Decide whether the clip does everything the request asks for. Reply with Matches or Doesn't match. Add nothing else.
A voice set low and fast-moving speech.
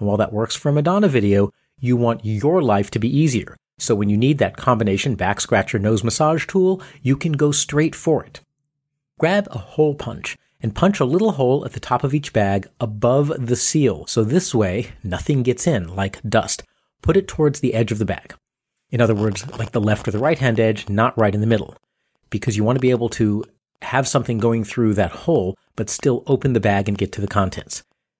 Matches